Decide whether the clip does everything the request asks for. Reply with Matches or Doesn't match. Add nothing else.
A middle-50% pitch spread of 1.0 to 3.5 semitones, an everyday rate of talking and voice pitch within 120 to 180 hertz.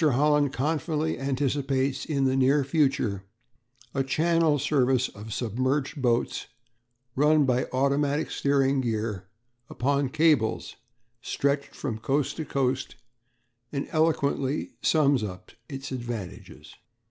Doesn't match